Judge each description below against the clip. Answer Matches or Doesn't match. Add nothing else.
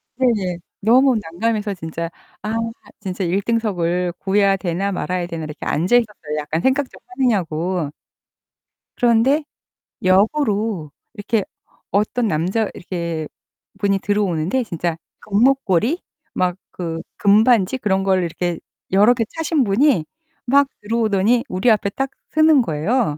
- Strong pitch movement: Doesn't match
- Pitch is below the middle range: Doesn't match